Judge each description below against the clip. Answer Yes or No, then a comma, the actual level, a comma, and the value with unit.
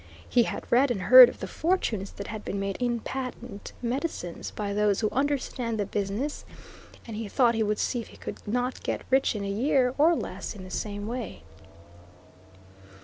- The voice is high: Yes, high, 230 Hz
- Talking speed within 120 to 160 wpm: No, average, 195 wpm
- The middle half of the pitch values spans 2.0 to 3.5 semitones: No, average, 3.9 semitones